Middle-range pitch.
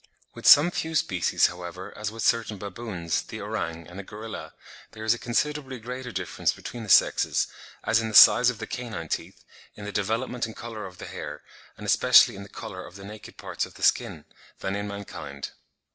No: low, 105 Hz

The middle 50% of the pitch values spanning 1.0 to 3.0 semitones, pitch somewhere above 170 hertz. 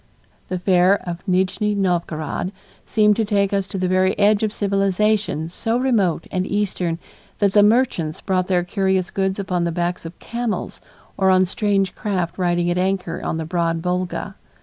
Yes: narrow, 2.4 semitones; high, 190 Hz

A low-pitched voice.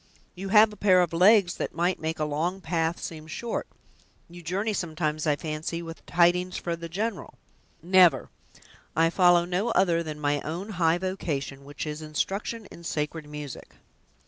No: medium, 170 Hz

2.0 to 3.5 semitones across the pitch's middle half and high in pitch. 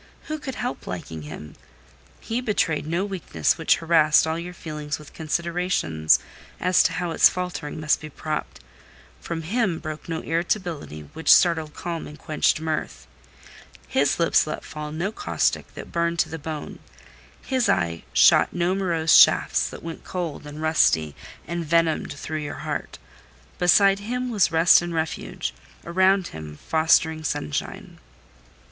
No: average, 2.8 semitones; medium, 160 Hz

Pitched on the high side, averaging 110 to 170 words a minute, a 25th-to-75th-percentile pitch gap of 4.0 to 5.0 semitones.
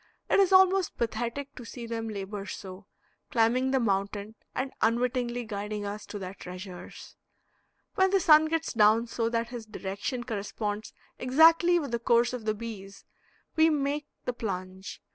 Yes: high, 230 Hz; average, 160 wpm; average, 4.3 semitones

